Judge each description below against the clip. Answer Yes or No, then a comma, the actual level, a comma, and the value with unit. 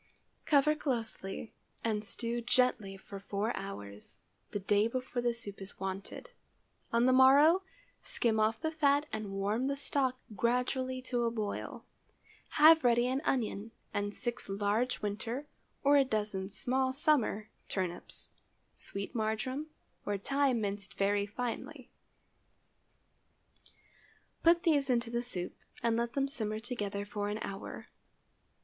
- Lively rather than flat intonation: No, average, 4.2 semitones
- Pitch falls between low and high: No, high, 235 Hz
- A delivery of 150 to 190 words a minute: No, slow, 135 wpm